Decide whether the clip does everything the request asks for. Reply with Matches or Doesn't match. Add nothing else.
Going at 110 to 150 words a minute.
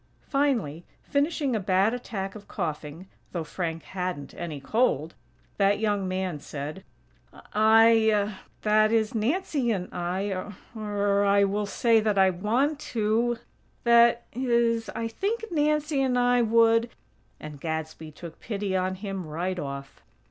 Matches